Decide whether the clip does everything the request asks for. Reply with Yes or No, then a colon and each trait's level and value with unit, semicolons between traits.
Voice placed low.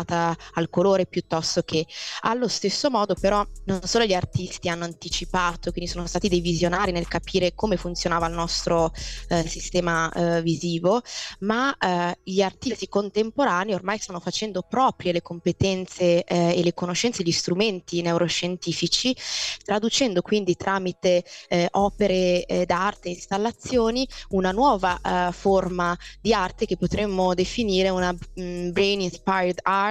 No: medium, 180 Hz